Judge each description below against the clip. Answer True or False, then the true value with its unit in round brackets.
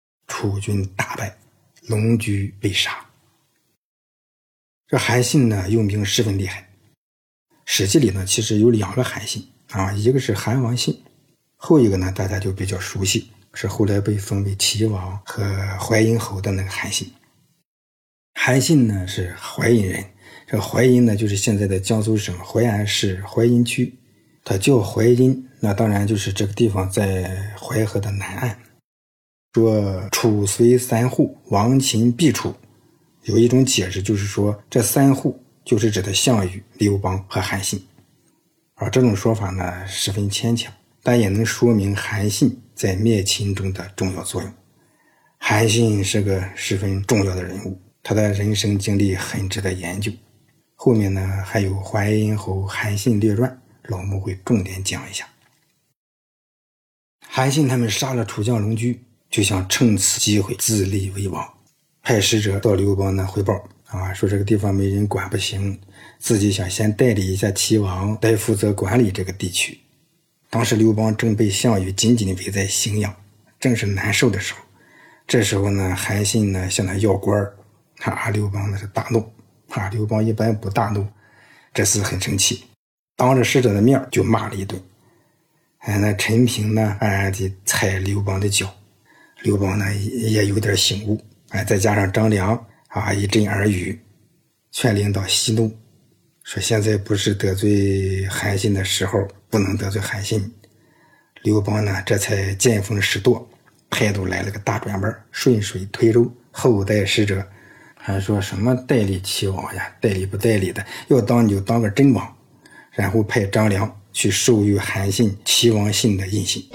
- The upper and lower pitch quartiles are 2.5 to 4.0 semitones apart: True (2.8 semitones)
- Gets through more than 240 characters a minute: False (230 characters per minute)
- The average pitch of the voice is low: True (105 Hz)